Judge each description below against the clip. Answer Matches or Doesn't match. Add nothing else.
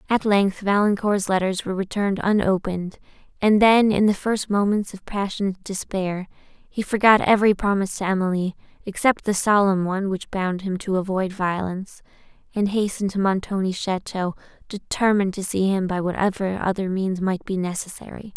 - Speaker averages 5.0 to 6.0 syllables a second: Matches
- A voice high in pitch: Matches